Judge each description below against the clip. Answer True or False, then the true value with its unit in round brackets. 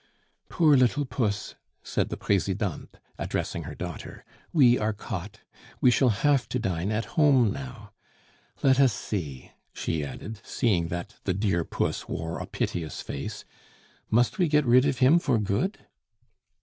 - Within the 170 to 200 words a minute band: False (150 wpm)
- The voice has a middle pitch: False (110 Hz)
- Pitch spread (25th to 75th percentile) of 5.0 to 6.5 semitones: True (5.4 semitones)